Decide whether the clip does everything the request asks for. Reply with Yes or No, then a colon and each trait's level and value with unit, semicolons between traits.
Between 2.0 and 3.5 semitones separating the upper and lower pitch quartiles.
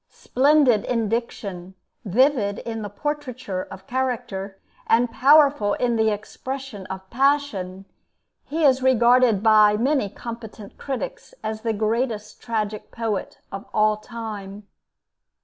No: average, 3.9 semitones